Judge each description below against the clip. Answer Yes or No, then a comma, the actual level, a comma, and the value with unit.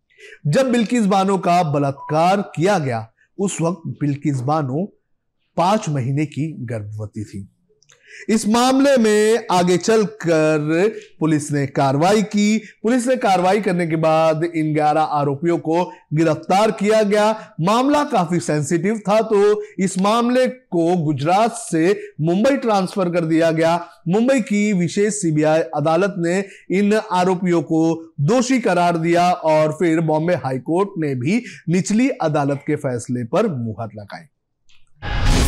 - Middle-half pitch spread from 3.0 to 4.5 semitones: No, wide, 5.4 semitones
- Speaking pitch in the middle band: Yes, medium, 175 Hz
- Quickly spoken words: No, average, 130 wpm